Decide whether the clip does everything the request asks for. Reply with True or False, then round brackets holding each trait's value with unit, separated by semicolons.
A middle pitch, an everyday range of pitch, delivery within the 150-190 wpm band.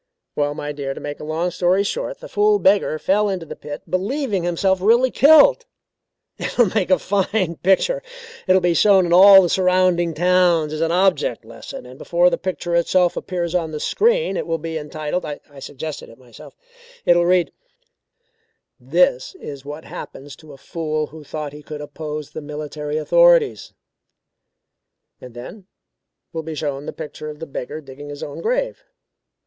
True (170 Hz; 4.1 semitones; 180 wpm)